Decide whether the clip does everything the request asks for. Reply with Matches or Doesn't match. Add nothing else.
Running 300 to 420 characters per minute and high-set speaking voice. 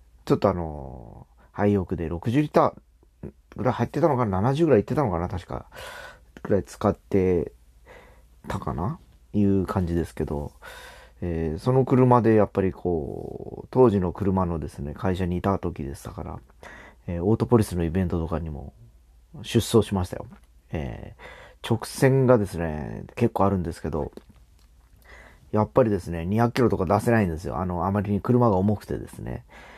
Doesn't match